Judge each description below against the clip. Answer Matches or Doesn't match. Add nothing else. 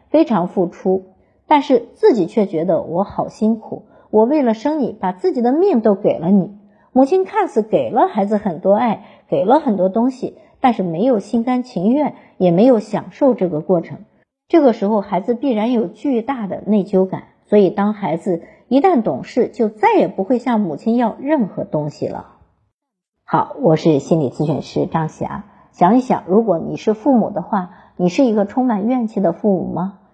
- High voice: Matches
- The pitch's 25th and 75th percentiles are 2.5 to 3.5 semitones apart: Doesn't match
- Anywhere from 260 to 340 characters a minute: Matches